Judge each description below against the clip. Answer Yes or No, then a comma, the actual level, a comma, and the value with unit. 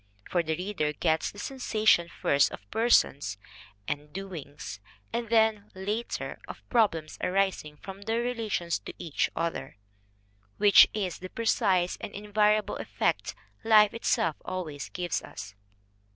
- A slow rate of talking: Yes, slow, 130 wpm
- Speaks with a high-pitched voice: Yes, high, 195 Hz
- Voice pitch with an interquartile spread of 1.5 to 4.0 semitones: No, average, 4.8 semitones